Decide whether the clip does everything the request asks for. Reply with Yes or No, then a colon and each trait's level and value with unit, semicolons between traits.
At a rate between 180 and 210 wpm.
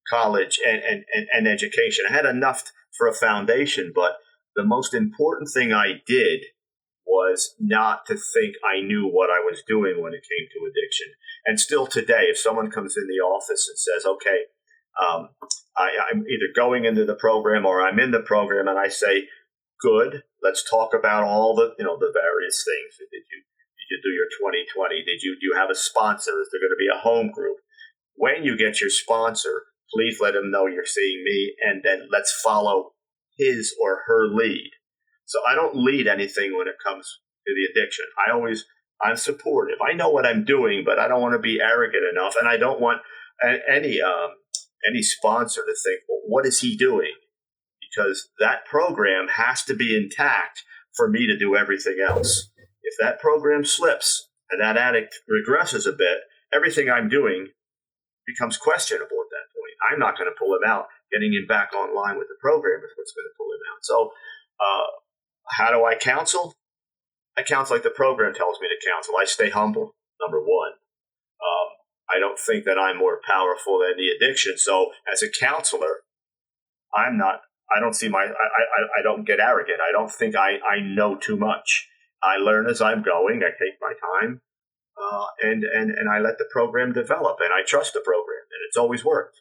Yes: average, 195 wpm